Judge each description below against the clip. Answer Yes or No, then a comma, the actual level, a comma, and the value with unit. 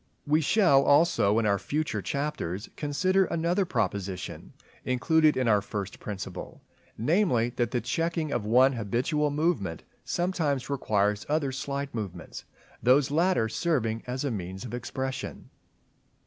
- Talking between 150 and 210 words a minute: No, slow, 135 wpm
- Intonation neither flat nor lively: No, wide, 6.0 semitones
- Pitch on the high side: No, low, 130 Hz